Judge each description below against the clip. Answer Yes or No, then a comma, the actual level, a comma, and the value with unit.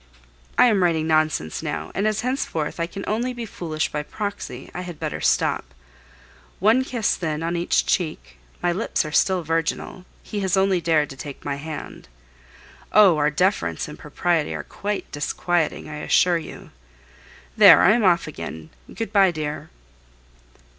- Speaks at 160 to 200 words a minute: Yes, average, 165 wpm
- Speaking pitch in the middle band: Yes, medium, 175 Hz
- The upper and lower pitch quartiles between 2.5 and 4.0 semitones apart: No, average, 4.5 semitones